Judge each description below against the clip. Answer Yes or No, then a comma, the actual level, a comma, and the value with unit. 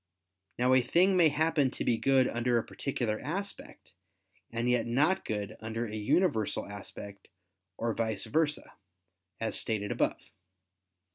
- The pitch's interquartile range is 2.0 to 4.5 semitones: No, average, 5.0 semitones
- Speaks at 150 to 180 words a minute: No, average, 140 wpm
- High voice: No, low, 120 Hz